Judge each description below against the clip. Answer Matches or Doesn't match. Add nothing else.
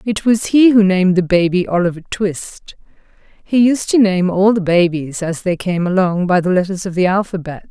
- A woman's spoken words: Matches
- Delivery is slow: Doesn't match